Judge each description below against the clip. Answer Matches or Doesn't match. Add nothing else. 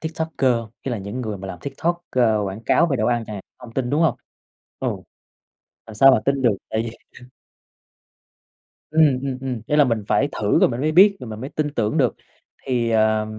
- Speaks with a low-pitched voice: Matches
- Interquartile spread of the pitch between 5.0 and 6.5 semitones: Doesn't match